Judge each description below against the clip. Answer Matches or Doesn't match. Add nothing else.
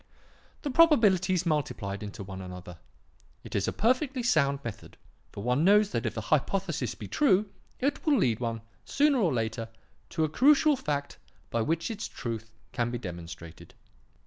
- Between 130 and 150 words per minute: Doesn't match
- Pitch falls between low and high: Matches